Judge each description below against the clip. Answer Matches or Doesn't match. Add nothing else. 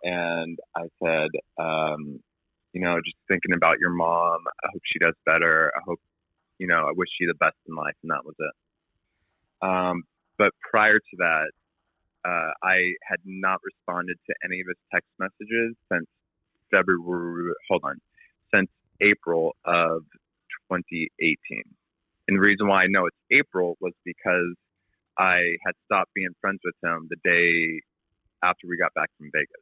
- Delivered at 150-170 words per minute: Matches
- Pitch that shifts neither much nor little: Doesn't match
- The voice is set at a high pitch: Doesn't match